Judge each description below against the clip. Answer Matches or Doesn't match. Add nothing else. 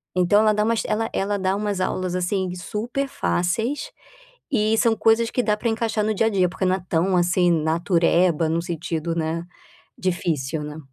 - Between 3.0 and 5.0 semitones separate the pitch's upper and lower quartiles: Matches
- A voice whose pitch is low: Doesn't match